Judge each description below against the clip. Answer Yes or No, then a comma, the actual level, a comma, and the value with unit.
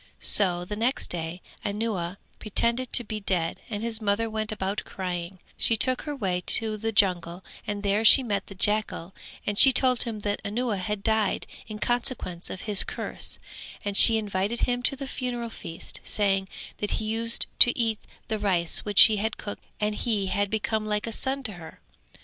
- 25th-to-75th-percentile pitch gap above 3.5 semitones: No, average, 2.7 semitones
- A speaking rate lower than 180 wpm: No, average, 190 wpm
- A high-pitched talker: Yes, high, 210 Hz